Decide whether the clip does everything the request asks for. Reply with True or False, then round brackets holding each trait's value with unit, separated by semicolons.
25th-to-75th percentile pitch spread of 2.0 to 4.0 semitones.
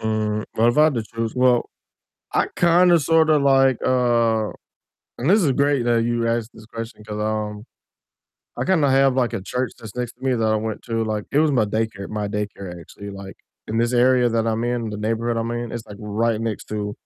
True (2.8 semitones)